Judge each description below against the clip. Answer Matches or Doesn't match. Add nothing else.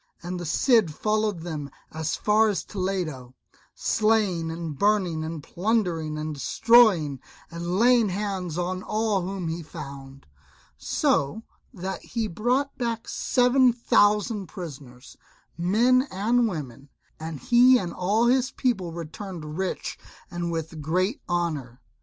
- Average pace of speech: Doesn't match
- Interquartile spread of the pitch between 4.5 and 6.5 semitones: Matches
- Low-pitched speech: Doesn't match